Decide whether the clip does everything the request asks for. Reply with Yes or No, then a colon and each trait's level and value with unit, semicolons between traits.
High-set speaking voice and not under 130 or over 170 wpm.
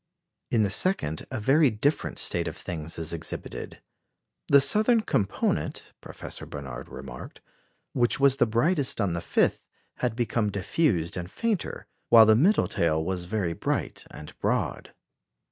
No: low, 105 Hz; average, 145 wpm